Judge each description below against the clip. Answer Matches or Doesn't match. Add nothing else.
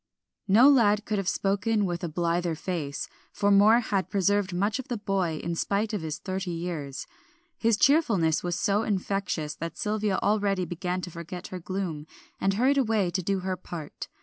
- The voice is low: Doesn't match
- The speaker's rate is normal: Matches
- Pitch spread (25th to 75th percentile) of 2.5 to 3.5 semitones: Matches